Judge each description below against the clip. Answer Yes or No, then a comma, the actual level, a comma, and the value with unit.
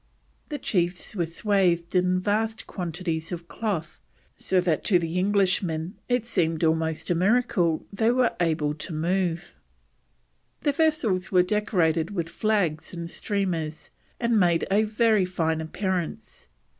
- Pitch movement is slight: No, average, 4.0 semitones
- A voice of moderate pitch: Yes, medium, 180 Hz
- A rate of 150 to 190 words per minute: No, slow, 135 wpm